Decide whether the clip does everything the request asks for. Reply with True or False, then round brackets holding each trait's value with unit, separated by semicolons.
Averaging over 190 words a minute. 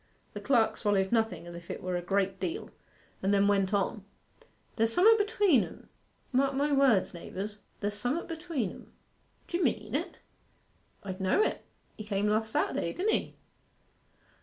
False (165 wpm)